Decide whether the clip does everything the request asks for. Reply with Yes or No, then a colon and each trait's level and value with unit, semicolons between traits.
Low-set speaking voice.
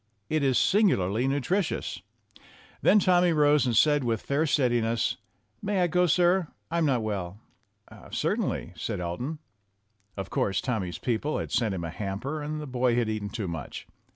Yes: low, 130 Hz